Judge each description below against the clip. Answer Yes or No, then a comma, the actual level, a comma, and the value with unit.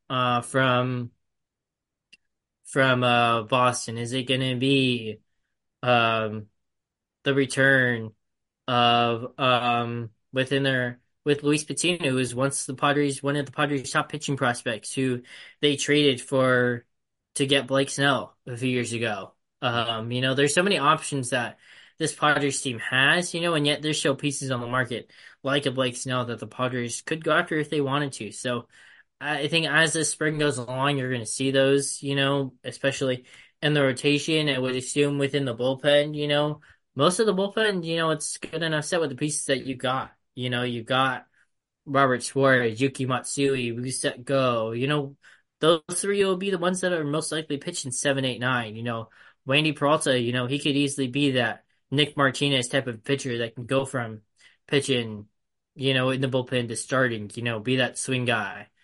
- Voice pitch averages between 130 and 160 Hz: Yes, low, 135 Hz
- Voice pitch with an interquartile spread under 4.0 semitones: Yes, average, 2.8 semitones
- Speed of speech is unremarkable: Yes, average, 190 wpm